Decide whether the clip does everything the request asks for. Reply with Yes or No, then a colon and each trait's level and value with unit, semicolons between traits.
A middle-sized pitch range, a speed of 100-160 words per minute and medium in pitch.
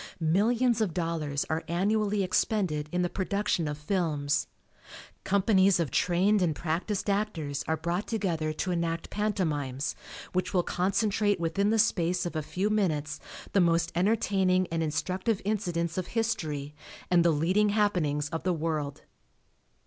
Yes: average, 4.0 semitones; average, 145 wpm; medium, 180 Hz